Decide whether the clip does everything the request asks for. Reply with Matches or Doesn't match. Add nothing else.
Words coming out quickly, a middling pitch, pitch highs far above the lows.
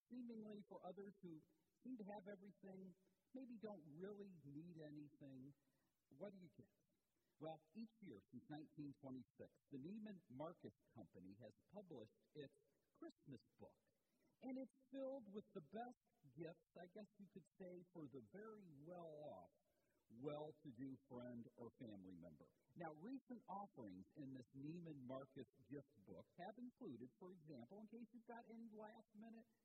Doesn't match